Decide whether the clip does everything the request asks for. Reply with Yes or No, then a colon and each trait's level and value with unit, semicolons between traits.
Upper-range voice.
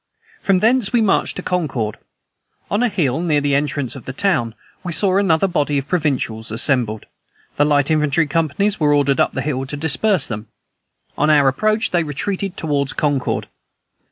No: medium, 150 Hz